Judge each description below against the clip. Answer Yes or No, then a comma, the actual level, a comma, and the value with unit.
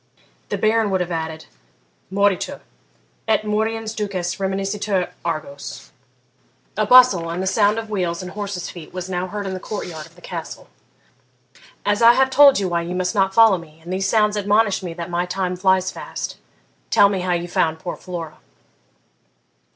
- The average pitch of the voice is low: No, high, 190 Hz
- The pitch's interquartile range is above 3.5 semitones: No, average, 3.0 semitones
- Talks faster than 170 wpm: Yes, average, 180 wpm